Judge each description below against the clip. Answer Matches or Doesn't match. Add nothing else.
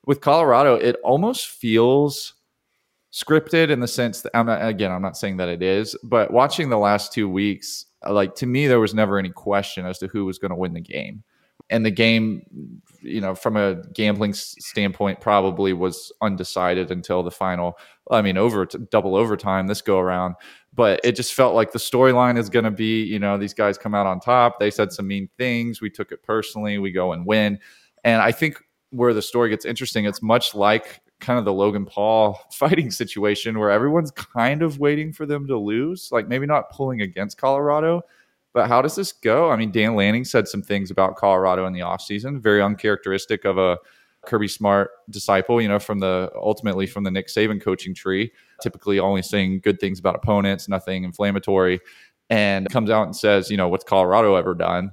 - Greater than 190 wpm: Matches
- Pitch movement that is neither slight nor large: Matches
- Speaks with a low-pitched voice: Matches